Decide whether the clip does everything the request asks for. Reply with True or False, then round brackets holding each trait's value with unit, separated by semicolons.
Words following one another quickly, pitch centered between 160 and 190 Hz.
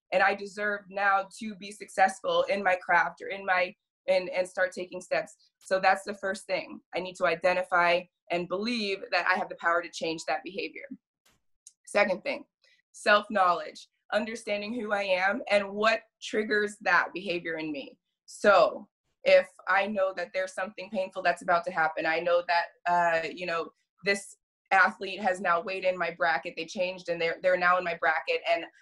False (180 wpm; 185 Hz)